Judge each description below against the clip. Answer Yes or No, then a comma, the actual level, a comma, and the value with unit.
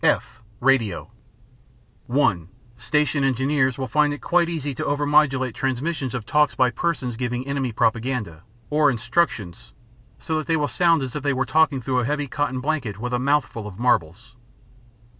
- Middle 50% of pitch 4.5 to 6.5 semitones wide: No, average, 3.5 semitones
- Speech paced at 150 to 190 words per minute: Yes, average, 170 wpm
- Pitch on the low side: Yes, low, 130 Hz